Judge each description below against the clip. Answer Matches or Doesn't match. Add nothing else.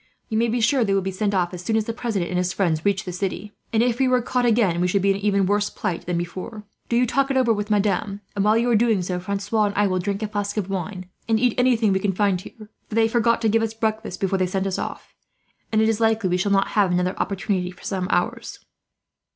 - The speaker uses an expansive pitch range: Doesn't match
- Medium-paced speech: Doesn't match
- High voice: Matches